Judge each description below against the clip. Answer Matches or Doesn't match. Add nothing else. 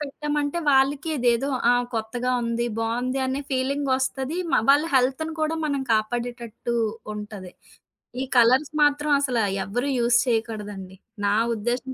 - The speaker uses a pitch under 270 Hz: Matches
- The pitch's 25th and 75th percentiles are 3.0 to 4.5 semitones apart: Matches